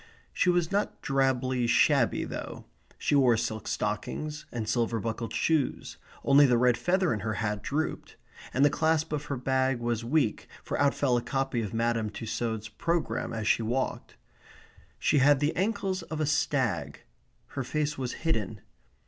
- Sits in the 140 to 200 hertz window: No, low, 130 Hz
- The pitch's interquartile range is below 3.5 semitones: No, average, 4.7 semitones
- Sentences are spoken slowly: No, average, 165 wpm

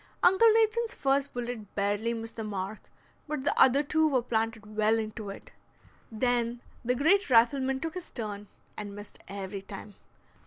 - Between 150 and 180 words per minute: Yes, average, 160 wpm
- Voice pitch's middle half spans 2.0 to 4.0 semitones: No, average, 4.7 semitones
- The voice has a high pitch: Yes, high, 235 Hz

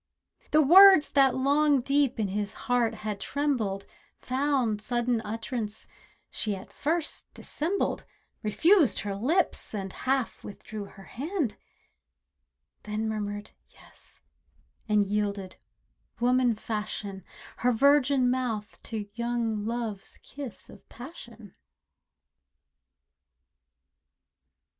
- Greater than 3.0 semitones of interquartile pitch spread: Yes, average, 4.6 semitones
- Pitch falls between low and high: No, high, 235 Hz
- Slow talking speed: Yes, slow, 100 wpm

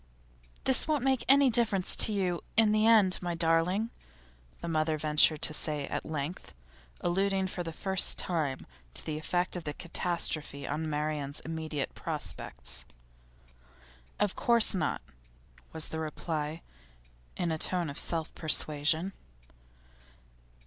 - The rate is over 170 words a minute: No, slow, 135 wpm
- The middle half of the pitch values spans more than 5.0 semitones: No, average, 3.8 semitones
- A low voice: No, medium, 165 Hz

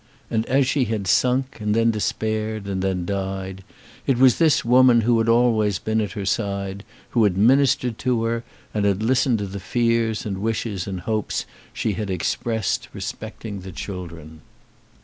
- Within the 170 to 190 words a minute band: Yes, average, 175 wpm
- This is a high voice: No, low, 110 Hz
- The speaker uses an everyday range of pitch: Yes, average, 3.1 semitones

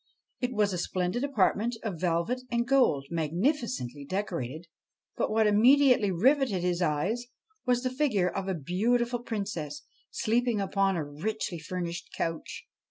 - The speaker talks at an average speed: Yes, average, 145 wpm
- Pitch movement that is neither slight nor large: No, wide, 6.0 semitones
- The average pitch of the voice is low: No, high, 200 Hz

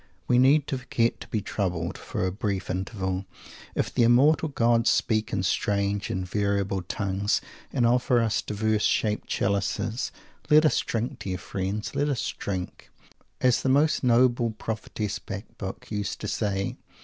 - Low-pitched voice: Yes, low, 110 Hz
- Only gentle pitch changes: No, average, 3.6 semitones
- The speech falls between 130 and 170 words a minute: Yes, average, 155 wpm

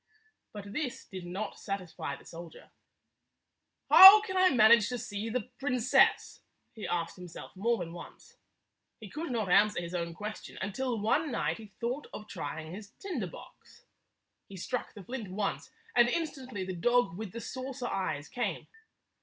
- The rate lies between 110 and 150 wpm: No, average, 165 wpm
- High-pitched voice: Yes, high, 215 Hz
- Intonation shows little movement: No, average, 5.1 semitones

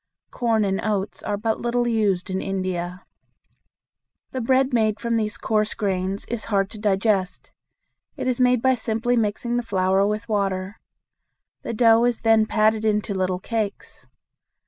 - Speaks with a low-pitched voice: No, high, 215 Hz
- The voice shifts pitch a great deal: No, average, 3.0 semitones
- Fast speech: No, average, 155 wpm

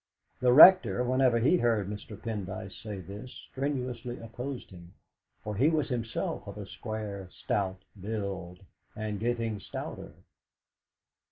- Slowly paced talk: Yes, slow, 125 wpm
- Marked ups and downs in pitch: No, average, 3.8 semitones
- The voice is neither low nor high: No, low, 110 Hz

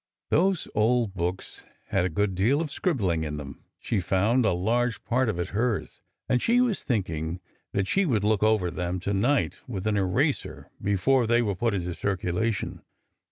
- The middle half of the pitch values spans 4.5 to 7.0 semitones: Yes, average, 4.9 semitones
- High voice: No, low, 105 Hz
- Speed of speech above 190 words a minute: No, average, 185 wpm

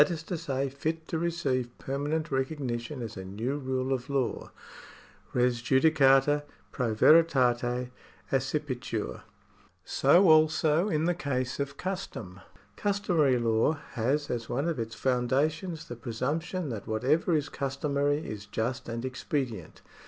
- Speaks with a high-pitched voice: No, low, 135 Hz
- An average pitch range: Yes, average, 4.1 semitones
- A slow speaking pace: Yes, slow, 130 wpm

